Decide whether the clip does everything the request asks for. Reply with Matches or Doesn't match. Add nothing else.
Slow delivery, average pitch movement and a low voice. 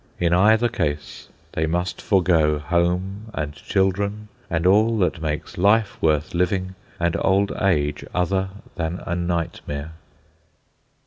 Matches